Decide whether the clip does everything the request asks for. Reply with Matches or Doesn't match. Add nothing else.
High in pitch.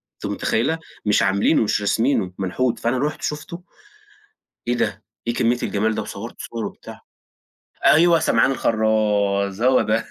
Doesn't match